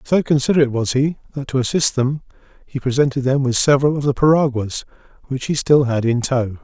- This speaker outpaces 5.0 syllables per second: Yes, 6.0 syllables/s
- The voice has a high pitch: No, low, 135 Hz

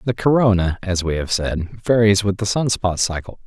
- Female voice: No, male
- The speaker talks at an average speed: No, fast, 210 wpm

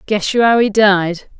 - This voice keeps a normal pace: No, fast, 215 wpm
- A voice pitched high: Yes, high, 205 Hz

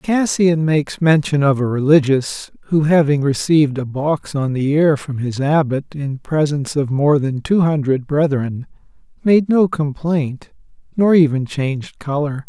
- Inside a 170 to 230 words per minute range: No, average, 155 wpm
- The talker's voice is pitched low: No, medium, 150 Hz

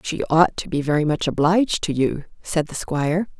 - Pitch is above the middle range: No, medium, 160 Hz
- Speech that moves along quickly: Yes, fast, 210 wpm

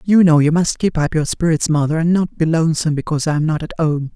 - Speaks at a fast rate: Yes, fast, 260 wpm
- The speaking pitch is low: No, medium, 160 Hz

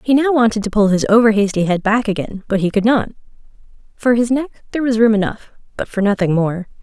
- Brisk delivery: Yes, fast, 230 wpm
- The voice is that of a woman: Yes, female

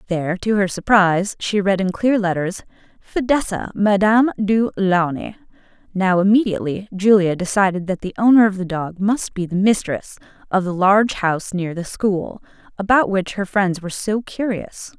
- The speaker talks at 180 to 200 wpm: No, average, 165 wpm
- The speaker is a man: No, female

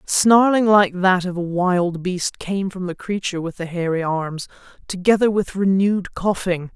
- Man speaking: No, female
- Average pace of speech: Yes, average, 170 wpm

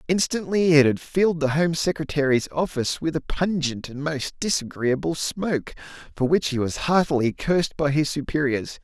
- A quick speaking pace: No, average, 165 wpm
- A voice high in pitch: No, medium, 150 Hz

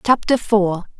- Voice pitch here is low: No, high, 205 Hz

